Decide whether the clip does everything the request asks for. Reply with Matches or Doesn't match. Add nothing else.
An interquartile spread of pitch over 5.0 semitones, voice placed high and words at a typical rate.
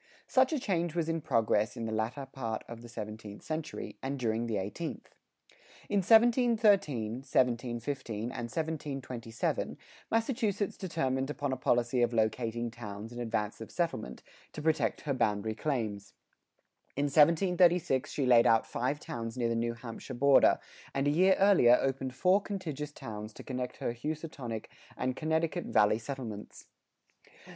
Doesn't match